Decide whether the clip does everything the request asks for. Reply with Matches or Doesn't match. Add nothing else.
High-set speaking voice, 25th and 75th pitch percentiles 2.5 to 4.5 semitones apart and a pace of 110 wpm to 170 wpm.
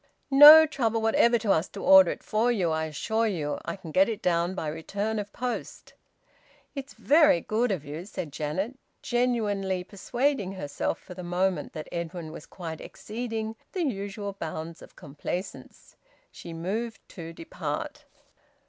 Doesn't match